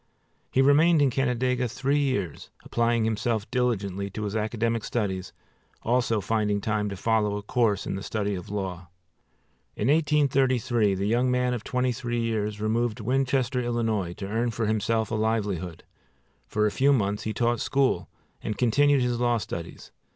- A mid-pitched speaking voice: No, low, 115 Hz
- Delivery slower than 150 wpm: No, average, 165 wpm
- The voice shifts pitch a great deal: No, average, 3.3 semitones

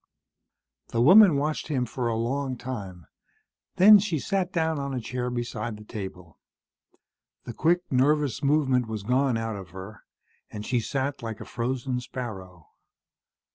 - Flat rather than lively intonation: No, average, 4.2 semitones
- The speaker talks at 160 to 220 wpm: No, average, 150 wpm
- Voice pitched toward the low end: Yes, low, 125 Hz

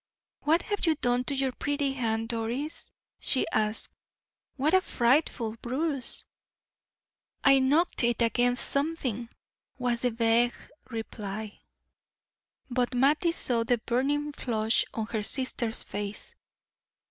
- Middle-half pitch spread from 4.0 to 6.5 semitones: No, average, 3.6 semitones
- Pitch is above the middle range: Yes, high, 245 Hz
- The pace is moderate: No, slow, 120 wpm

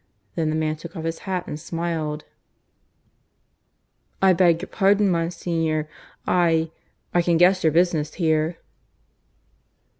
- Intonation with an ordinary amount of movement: No, narrow, 1.9 semitones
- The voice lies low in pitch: No, medium, 165 Hz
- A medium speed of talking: No, slow, 125 wpm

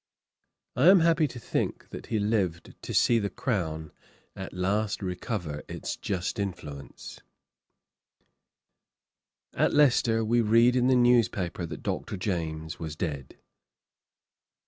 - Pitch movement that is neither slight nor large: No, wide, 5.9 semitones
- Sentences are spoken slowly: Yes, slow, 125 wpm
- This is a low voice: Yes, low, 100 Hz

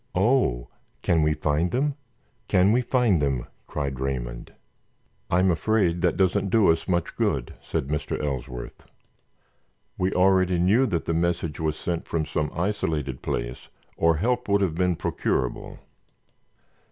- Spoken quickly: No, average, 140 wpm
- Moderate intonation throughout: Yes, average, 4.4 semitones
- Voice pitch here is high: No, very low, 85 Hz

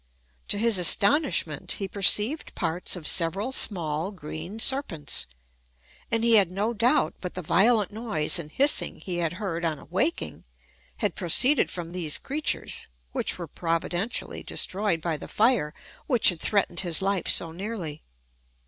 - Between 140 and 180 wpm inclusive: Yes, average, 150 wpm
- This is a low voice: No, high, 190 Hz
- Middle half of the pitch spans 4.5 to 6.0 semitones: Yes, average, 5.1 semitones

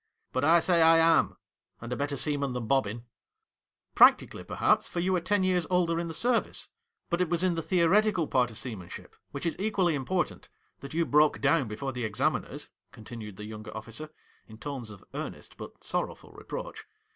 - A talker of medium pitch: Yes, medium, 150 Hz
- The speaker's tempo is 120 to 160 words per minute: No, fast, 205 wpm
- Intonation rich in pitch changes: Yes, wide, 6.3 semitones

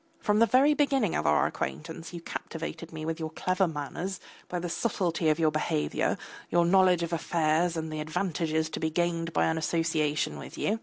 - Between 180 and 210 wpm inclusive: Yes, average, 190 wpm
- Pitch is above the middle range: No, medium, 165 Hz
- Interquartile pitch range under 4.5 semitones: Yes, narrow, 2.5 semitones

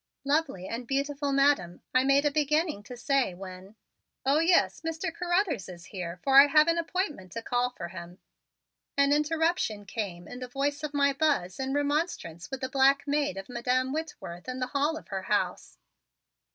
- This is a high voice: Yes, very high, 275 Hz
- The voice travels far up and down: Yes, wide, 6.2 semitones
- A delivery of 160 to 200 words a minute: Yes, average, 180 wpm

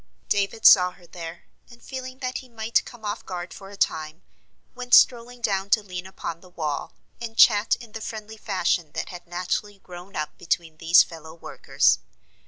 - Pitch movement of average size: Yes, average, 4.4 semitones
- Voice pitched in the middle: No, high, 195 Hz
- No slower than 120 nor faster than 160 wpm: No, average, 190 wpm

